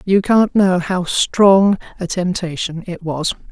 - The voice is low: No, medium, 185 Hz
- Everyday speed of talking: Yes, average, 155 wpm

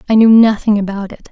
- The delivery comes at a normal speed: No, fast, 230 wpm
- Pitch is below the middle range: No, high, 210 Hz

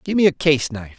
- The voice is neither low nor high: Yes, medium, 145 Hz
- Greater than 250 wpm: No, fast, 245 wpm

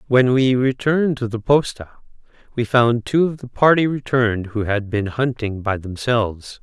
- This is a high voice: No, low, 120 Hz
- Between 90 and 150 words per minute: No, average, 170 wpm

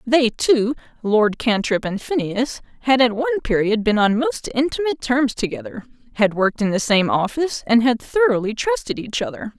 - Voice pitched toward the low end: No, high, 240 Hz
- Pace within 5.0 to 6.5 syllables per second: Yes, 5.3 syllables/s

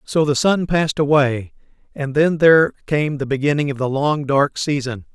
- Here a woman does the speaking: No, male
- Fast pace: No, average, 185 wpm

